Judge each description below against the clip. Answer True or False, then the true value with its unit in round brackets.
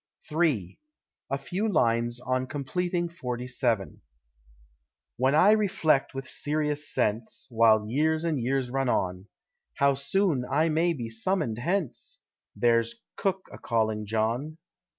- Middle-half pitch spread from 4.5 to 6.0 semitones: True (5.4 semitones)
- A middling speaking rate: False (130 wpm)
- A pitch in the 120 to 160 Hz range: True (135 Hz)